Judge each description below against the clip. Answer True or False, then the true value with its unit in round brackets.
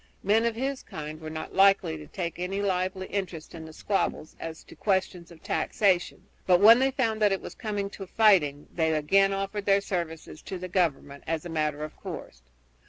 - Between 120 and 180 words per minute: False (200 wpm)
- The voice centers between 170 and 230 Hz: True (185 Hz)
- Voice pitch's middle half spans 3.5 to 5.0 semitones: True (3.9 semitones)